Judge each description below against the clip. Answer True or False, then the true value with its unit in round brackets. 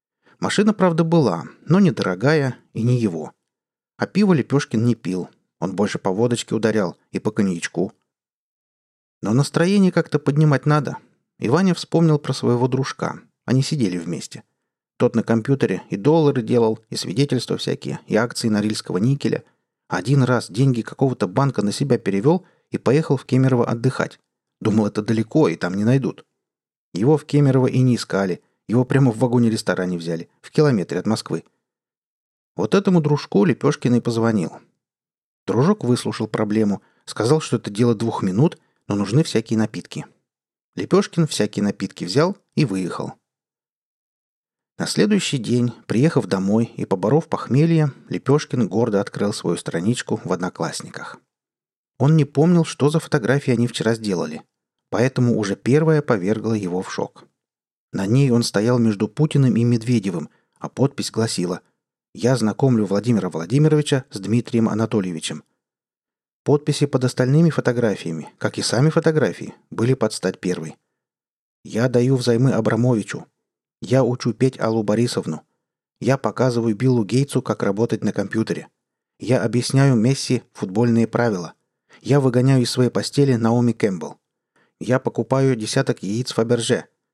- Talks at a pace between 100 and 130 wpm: False (140 wpm)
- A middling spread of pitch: True (4.1 semitones)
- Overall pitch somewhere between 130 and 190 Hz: False (120 Hz)